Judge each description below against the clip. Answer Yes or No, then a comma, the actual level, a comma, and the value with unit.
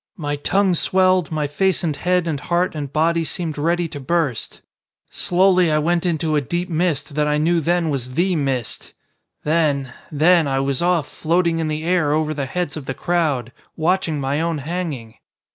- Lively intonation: No, average, 3.2 semitones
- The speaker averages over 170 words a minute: Yes, average, 185 wpm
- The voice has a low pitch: No, medium, 160 Hz